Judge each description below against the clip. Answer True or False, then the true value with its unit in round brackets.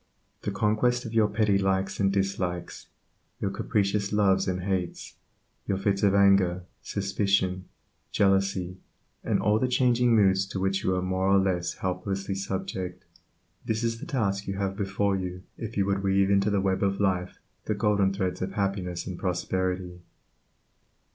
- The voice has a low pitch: True (95 Hz)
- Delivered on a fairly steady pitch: True (1.4 semitones)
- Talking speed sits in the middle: True (160 wpm)